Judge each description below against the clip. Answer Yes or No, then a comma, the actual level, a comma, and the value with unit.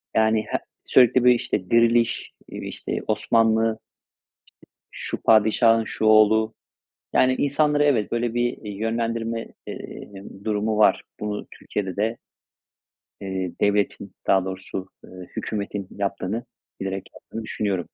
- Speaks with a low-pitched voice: Yes, low, 110 Hz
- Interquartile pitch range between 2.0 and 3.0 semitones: Yes, narrow, 2.4 semitones